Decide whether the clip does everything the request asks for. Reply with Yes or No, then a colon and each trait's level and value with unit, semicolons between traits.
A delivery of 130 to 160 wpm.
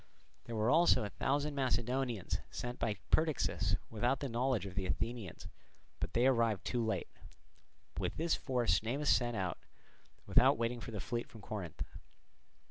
Yes: average, 155 wpm